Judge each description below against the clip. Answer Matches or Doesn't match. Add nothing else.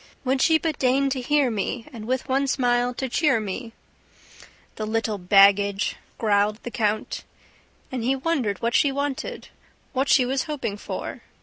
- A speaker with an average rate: Matches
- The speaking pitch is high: Matches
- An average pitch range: Matches